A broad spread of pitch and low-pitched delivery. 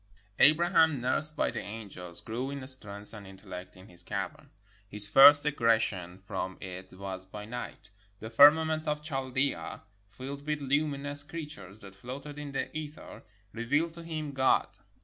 Yes: wide, 6.6 semitones; low, 130 Hz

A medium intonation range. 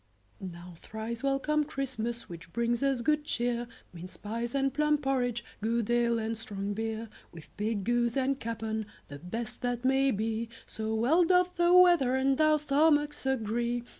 Yes: average, 3.8 semitones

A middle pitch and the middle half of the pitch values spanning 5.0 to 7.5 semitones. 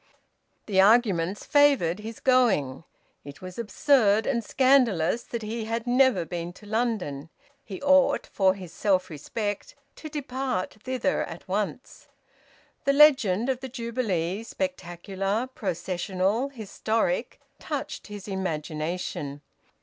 No: high, 210 Hz; wide, 5.5 semitones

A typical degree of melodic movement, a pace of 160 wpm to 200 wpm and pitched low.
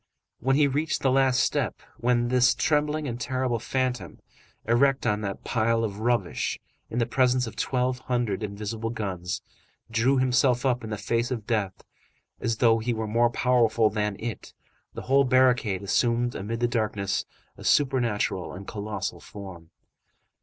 Yes: average, 3.2 semitones; average, 165 wpm; low, 120 Hz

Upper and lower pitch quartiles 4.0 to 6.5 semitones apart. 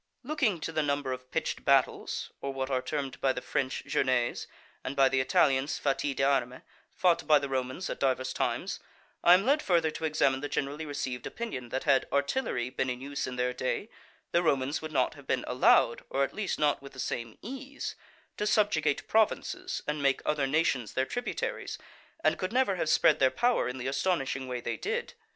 Yes: average, 4.8 semitones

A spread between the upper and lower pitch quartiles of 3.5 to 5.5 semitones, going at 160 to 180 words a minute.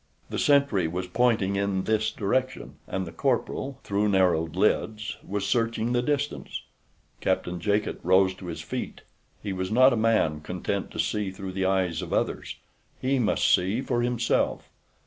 Yes: average, 4.0 semitones; average, 165 wpm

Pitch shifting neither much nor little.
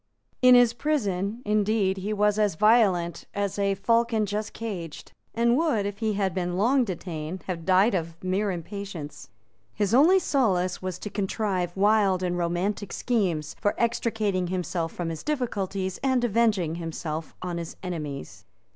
Yes: average, 3.7 semitones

